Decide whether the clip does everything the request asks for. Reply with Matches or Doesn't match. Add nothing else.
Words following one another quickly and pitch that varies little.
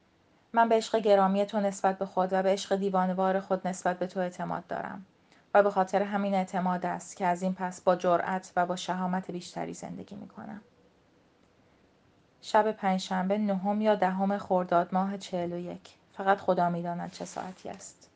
Matches